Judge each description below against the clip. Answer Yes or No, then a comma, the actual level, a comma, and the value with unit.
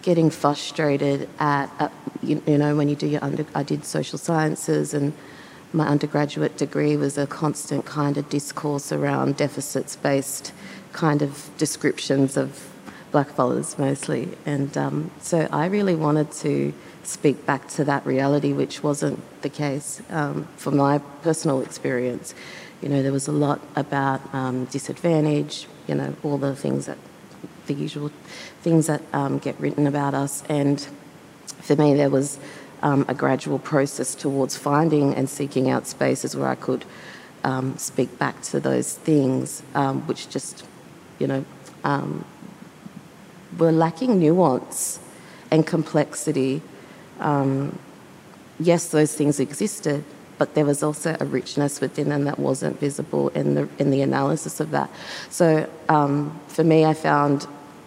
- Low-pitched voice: No, medium, 145 Hz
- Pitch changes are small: Yes, narrow, 1.7 semitones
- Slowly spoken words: No, average, 150 wpm